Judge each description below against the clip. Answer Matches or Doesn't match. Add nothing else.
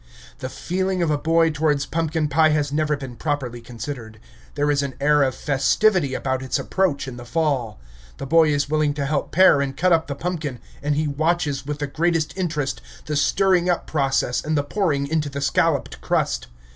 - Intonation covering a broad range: Doesn't match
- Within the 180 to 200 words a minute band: Matches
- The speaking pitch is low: Doesn't match